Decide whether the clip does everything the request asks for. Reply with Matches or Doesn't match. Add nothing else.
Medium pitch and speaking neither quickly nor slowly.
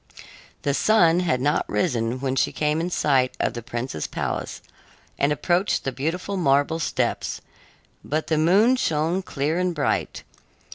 Matches